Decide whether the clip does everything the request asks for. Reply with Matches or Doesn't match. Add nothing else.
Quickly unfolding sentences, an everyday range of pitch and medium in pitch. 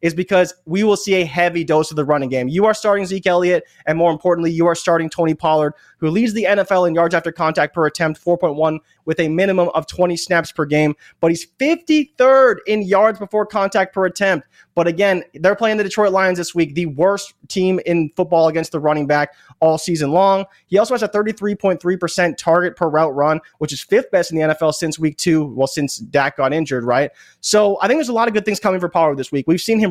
Matches